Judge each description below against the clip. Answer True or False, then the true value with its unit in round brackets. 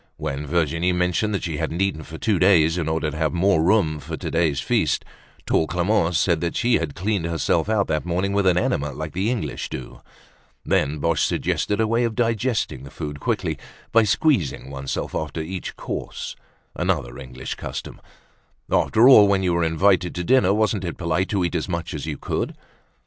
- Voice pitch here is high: False (85 Hz)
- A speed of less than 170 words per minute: False (190 wpm)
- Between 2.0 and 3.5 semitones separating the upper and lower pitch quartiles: False (4.2 semitones)